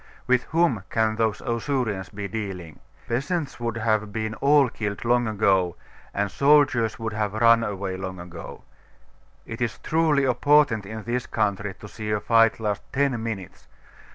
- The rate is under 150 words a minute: No, average, 160 wpm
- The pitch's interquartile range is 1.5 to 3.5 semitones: Yes, average, 3.2 semitones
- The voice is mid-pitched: No, low, 110 Hz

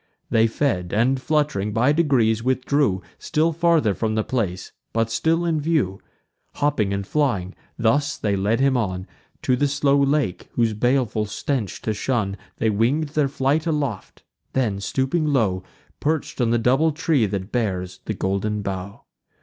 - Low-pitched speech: Yes, low, 120 Hz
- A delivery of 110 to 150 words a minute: No, average, 160 wpm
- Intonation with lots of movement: Yes, wide, 5.8 semitones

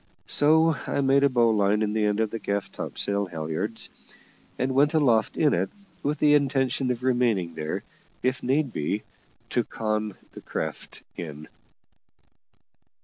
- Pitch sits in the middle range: No, low, 115 Hz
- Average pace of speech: Yes, average, 145 wpm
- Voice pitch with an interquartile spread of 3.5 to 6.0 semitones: Yes, average, 5.1 semitones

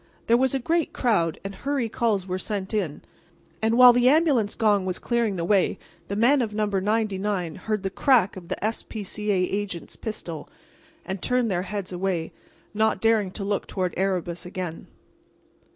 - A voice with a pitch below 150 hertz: No, high, 205 Hz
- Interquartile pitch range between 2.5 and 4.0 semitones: Yes, average, 3.5 semitones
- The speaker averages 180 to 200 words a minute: Yes, average, 185 wpm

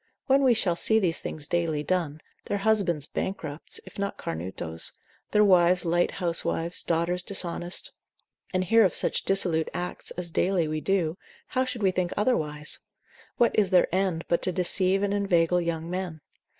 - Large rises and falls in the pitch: No, average, 3.0 semitones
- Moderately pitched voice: Yes, medium, 180 Hz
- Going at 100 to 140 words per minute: No, average, 165 wpm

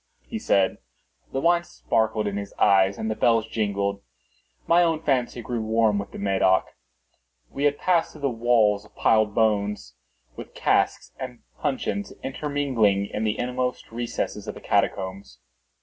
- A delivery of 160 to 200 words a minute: No, average, 150 wpm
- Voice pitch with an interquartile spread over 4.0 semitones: Yes, average, 4.7 semitones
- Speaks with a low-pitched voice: Yes, low, 110 Hz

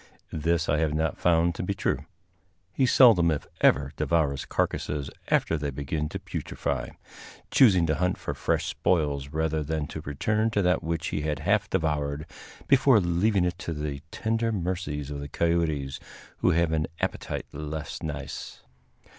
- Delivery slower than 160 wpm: No, average, 165 wpm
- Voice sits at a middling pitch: No, very low, 80 Hz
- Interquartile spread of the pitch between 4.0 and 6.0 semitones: No, average, 3.3 semitones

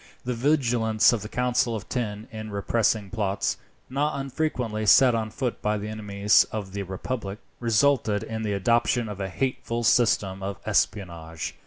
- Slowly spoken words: No, average, 160 wpm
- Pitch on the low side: Yes, low, 110 Hz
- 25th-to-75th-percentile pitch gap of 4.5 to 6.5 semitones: No, average, 3.2 semitones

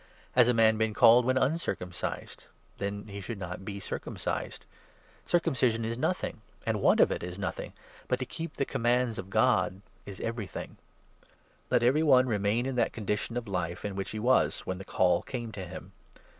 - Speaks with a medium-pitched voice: No, low, 110 Hz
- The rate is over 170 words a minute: Yes, average, 190 wpm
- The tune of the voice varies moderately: Yes, average, 4.2 semitones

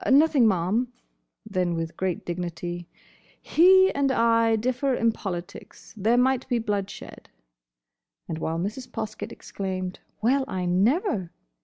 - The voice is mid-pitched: No, high, 215 Hz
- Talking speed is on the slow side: Yes, slow, 125 wpm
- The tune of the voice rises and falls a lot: Yes, wide, 5.8 semitones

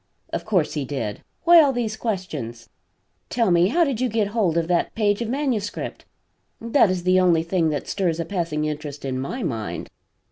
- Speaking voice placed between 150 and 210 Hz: Yes, medium, 185 Hz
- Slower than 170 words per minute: No, average, 190 wpm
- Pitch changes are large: Yes, wide, 6.6 semitones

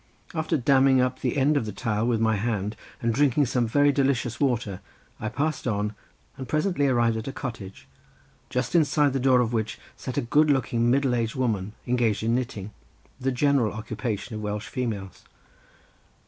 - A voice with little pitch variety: No, average, 3.5 semitones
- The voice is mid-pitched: No, low, 120 Hz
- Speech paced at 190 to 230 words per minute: No, average, 175 wpm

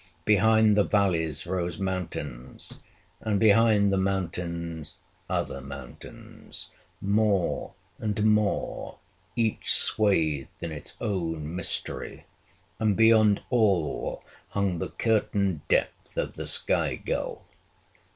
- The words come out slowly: Yes, slow, 100 wpm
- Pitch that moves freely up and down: No, average, 4.2 semitones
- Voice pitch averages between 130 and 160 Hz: No, low, 100 Hz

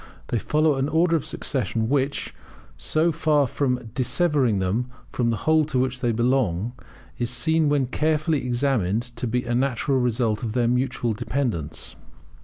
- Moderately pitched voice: No, low, 125 Hz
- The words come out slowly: No, average, 160 wpm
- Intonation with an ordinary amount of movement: Yes, average, 3.7 semitones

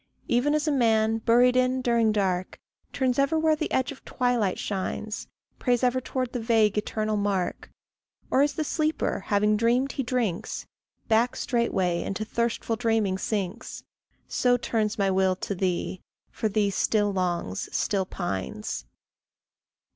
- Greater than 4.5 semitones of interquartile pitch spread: No, average, 4.0 semitones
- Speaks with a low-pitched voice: No, high, 225 Hz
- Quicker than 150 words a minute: No, average, 145 wpm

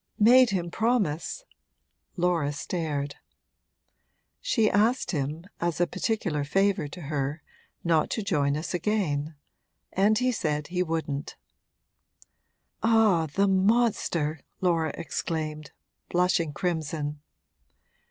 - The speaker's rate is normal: No, slow, 105 wpm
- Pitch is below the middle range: No, medium, 170 Hz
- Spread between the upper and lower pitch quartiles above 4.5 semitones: Yes, average, 5.0 semitones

